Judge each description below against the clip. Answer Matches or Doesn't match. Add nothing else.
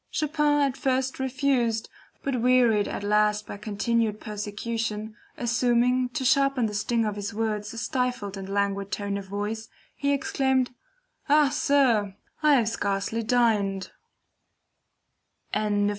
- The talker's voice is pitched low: Doesn't match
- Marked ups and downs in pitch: Doesn't match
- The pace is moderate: Doesn't match